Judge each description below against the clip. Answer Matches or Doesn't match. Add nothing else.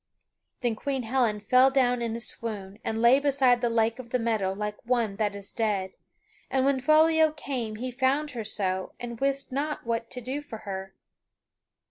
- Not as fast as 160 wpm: Doesn't match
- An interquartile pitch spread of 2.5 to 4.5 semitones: Matches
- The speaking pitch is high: Matches